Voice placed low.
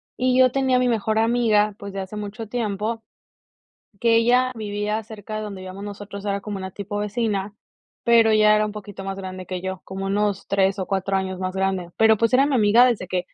No: high, 210 Hz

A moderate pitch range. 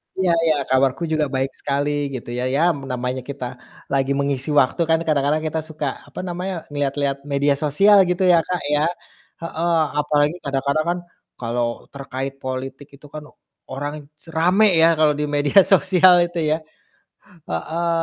Yes: average, 3.3 semitones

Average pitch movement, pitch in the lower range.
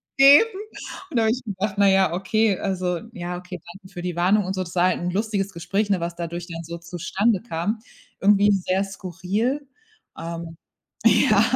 No: average, 3.0 semitones; high, 190 Hz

